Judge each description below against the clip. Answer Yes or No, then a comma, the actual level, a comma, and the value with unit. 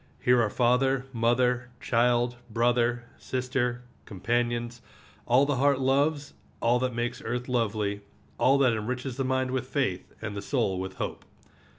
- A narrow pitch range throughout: Yes, narrow, 1.7 semitones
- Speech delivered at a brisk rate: No, average, 150 wpm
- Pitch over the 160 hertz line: No, low, 120 Hz